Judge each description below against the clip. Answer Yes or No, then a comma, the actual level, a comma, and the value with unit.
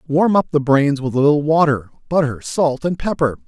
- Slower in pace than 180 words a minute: No, fast, 205 wpm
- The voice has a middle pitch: Yes, medium, 145 Hz